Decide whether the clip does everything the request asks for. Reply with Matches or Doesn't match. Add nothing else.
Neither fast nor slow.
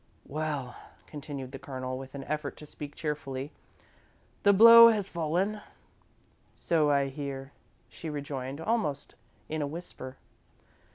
Doesn't match